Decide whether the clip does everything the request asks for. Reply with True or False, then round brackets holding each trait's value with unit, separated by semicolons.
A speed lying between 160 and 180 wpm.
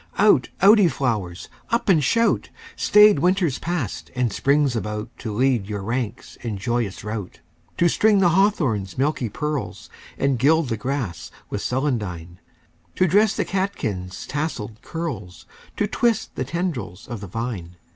False (150 wpm)